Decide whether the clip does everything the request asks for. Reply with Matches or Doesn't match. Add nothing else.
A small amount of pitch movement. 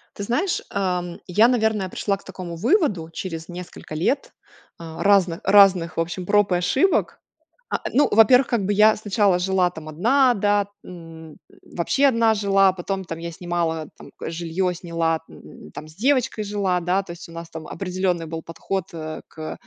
Doesn't match